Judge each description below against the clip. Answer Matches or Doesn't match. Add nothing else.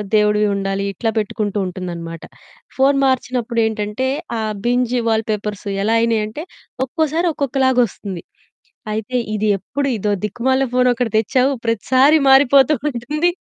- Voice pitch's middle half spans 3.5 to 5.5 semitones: Matches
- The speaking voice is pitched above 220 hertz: Matches